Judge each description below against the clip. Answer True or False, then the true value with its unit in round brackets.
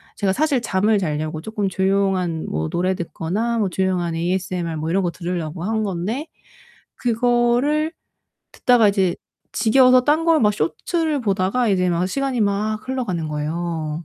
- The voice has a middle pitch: False (195 Hz)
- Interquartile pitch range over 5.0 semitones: True (5.6 semitones)